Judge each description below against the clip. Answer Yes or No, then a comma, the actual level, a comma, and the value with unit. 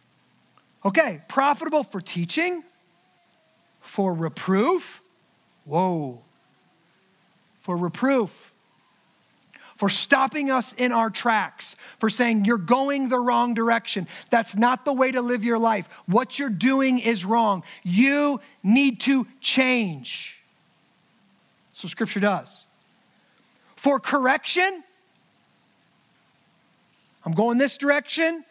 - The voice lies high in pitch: Yes, high, 235 Hz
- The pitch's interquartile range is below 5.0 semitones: No, average, 5.3 semitones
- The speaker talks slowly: Yes, slow, 100 wpm